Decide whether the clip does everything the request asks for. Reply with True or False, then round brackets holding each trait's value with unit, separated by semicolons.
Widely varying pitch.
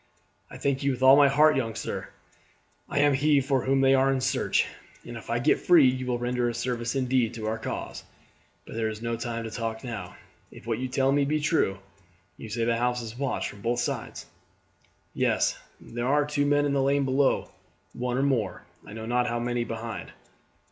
False (2.8 semitones)